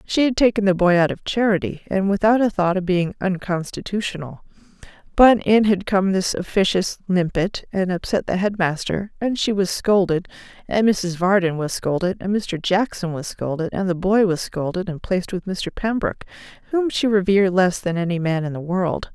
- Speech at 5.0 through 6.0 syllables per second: Yes, 5.1 syllables/s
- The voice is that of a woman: Yes, female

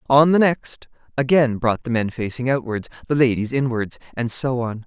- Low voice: Yes, low, 125 Hz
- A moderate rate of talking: Yes, average, 160 wpm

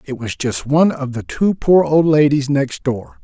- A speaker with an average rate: No, fast, 225 wpm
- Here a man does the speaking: Yes, male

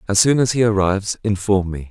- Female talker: No, male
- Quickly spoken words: Yes, fast, 220 wpm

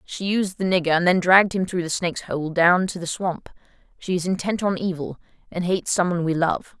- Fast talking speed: Yes, fast, 240 wpm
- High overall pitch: No, medium, 180 Hz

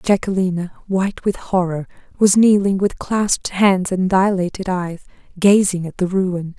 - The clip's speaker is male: No, female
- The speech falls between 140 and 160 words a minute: Yes, average, 145 wpm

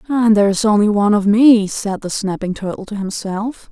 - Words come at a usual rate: No, fast, 210 wpm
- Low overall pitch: No, high, 205 Hz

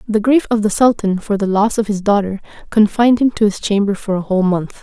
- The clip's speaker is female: Yes, female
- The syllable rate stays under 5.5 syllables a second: No, 6.0 syllables/s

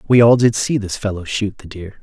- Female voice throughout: No, male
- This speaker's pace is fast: Yes, fast, 265 wpm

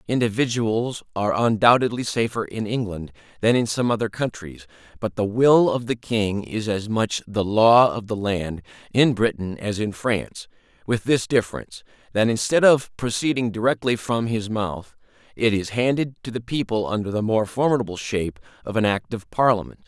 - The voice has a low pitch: Yes, low, 110 Hz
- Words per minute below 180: Yes, average, 170 wpm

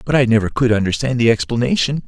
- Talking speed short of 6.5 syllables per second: No, 6.8 syllables/s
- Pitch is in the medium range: No, low, 120 Hz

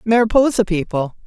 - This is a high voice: Yes, high, 205 Hz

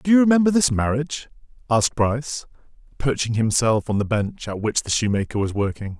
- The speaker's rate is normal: Yes, average, 180 wpm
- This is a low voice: Yes, low, 125 Hz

